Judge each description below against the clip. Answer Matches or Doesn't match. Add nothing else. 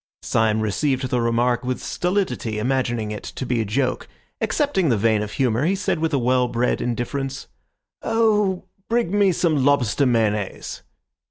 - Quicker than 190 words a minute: Doesn't match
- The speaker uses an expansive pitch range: Matches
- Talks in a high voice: Doesn't match